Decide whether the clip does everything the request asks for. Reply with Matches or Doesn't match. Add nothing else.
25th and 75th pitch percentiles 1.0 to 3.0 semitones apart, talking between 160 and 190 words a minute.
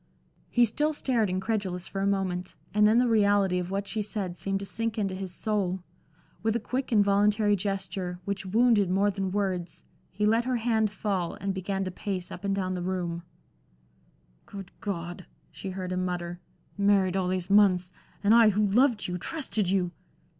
Matches